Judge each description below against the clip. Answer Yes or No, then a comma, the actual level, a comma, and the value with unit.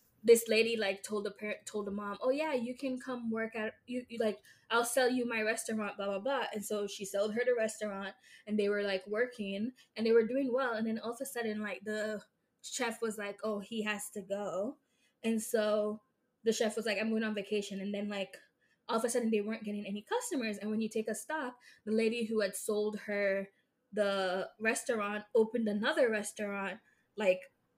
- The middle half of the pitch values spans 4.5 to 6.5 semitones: No, narrow, 2.5 semitones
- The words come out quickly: Yes, fast, 215 wpm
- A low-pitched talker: No, high, 220 Hz